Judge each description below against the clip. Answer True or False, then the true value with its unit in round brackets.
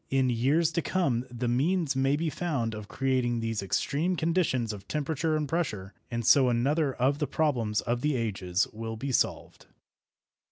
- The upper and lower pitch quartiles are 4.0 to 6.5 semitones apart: True (4.8 semitones)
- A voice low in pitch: True (130 Hz)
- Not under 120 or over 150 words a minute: False (170 wpm)